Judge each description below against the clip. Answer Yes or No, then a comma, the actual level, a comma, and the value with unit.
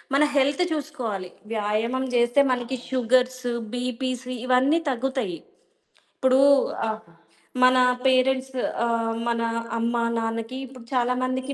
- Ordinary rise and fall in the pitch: No, narrow, 2.1 semitones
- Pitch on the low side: No, very high, 255 Hz